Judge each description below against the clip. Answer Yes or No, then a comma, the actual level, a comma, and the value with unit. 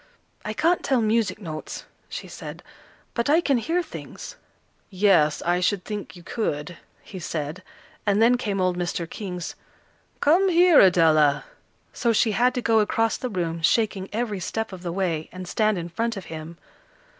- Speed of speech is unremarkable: Yes, average, 170 wpm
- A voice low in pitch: No, high, 200 Hz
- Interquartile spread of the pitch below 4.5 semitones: No, average, 4.9 semitones